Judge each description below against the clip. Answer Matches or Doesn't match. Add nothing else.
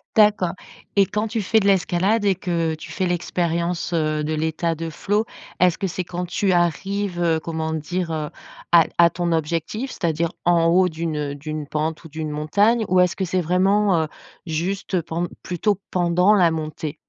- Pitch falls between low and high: Matches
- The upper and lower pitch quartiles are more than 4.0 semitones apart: Doesn't match